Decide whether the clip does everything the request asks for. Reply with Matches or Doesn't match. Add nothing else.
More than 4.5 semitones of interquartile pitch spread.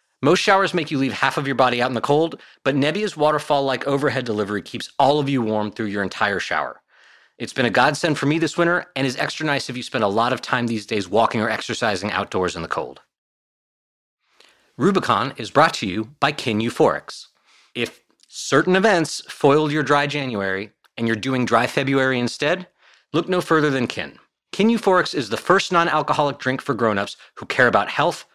Doesn't match